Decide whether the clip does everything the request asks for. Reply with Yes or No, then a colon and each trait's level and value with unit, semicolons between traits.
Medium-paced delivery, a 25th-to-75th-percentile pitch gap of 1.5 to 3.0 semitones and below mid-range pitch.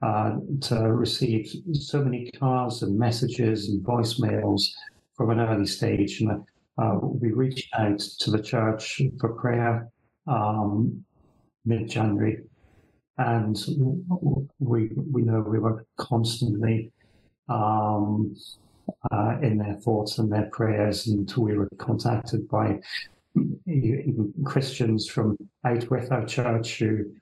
No: slow, 115 wpm; average, 2.7 semitones; low, 115 Hz